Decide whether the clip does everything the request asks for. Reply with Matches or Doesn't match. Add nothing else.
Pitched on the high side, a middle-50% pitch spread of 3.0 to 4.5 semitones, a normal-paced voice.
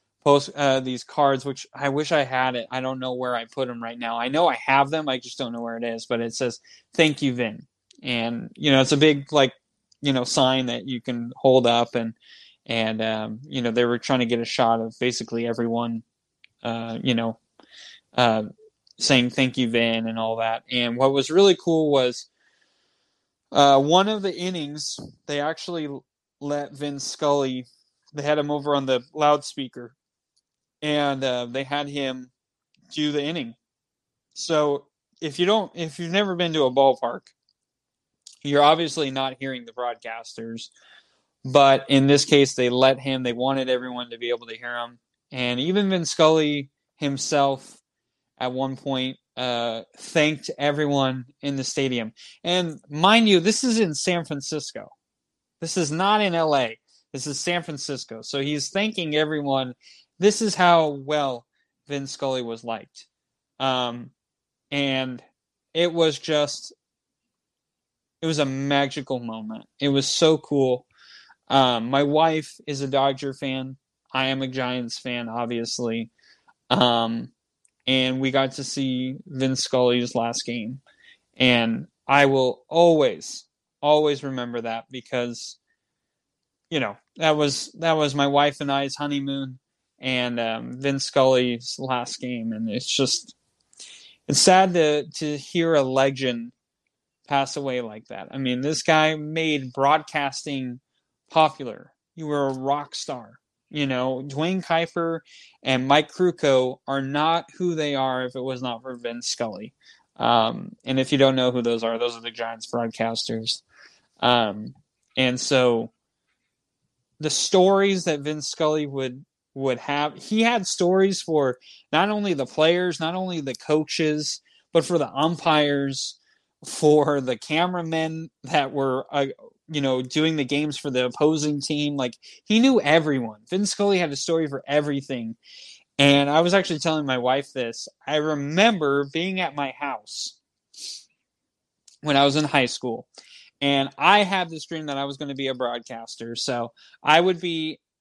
Doesn't match